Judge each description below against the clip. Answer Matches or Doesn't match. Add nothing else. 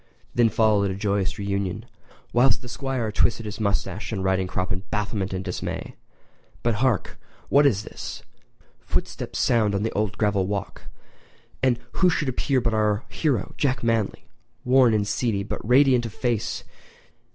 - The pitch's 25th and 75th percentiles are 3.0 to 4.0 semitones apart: Matches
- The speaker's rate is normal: Matches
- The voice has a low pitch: Matches